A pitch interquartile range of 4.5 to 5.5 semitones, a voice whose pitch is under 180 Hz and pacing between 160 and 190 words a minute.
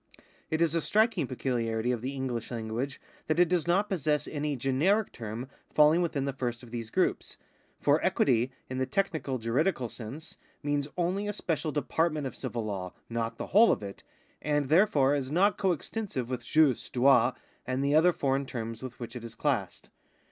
Yes: average, 4.8 semitones; low, 135 Hz; average, 185 wpm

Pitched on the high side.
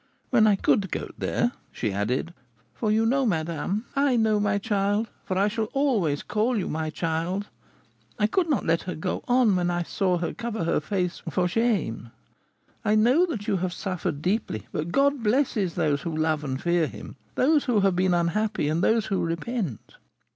Yes: high, 195 Hz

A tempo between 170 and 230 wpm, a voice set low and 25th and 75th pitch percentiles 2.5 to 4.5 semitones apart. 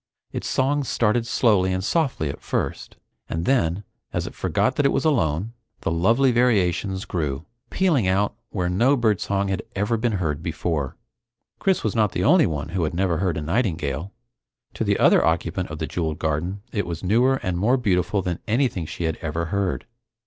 No: average, 185 wpm; very low, 95 Hz; wide, 5.6 semitones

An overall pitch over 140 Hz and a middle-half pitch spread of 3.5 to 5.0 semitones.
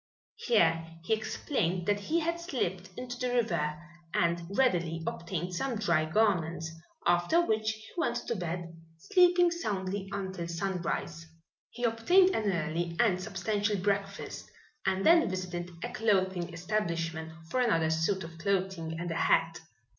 Yes: high, 190 Hz; average, 4.7 semitones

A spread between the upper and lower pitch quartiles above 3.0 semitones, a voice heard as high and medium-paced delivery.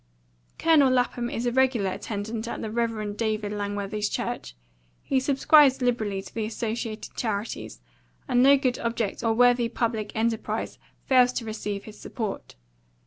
No: average, 2.7 semitones; high, 230 Hz; average, 145 wpm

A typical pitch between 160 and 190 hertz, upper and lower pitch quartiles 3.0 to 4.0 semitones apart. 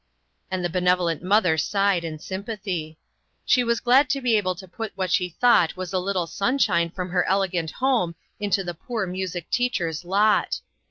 Yes: medium, 185 Hz; average, 3.4 semitones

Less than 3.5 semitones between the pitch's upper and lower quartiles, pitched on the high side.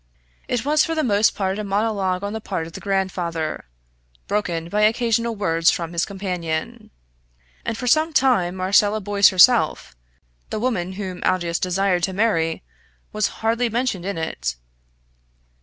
No: average, 4.0 semitones; high, 195 Hz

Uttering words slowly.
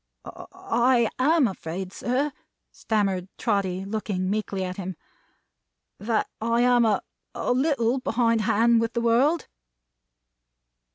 Yes: slow, 115 wpm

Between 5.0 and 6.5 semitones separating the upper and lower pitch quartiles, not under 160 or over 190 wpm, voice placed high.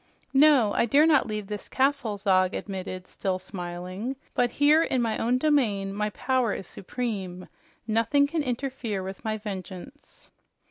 No: wide, 5.5 semitones; average, 150 wpm; high, 220 Hz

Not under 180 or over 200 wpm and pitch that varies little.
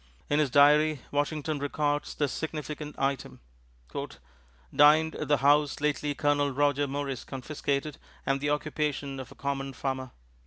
No: average, 140 wpm; narrow, 1.4 semitones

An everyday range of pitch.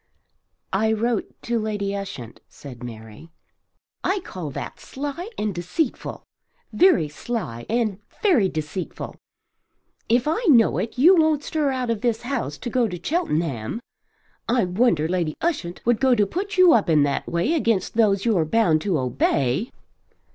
No: wide, 7.3 semitones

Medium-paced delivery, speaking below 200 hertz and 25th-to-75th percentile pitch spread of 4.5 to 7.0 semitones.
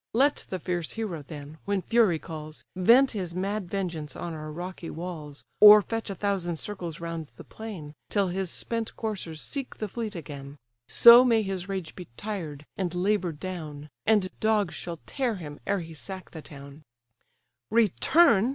Yes: average, 170 wpm; medium, 185 Hz; average, 4.8 semitones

